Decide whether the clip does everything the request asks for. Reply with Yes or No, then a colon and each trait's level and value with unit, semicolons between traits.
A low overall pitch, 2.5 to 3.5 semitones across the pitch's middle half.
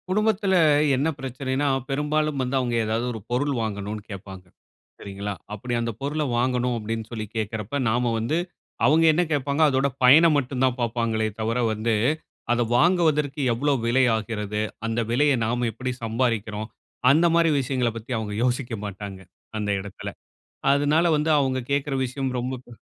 No: low, 125 Hz; average, 4.3 semitones